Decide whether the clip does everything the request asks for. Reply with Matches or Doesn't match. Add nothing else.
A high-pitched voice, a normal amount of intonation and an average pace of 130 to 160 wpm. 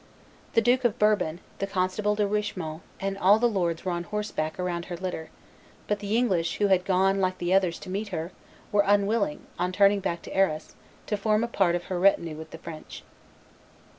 Doesn't match